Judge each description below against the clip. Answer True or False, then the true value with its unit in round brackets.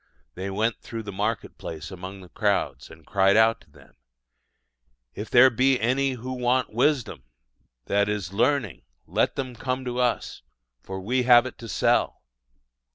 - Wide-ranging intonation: False (4.5 semitones)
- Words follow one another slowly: False (160 wpm)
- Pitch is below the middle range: True (115 Hz)